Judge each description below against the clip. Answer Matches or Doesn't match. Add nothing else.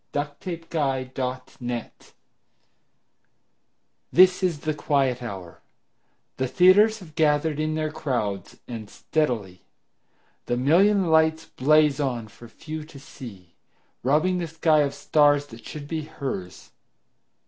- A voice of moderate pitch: Matches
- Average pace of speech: Doesn't match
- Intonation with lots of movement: Doesn't match